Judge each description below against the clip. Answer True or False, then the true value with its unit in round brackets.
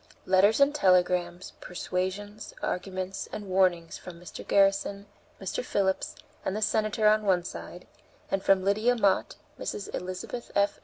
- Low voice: False (195 Hz)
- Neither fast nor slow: True (145 wpm)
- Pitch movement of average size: False (2.2 semitones)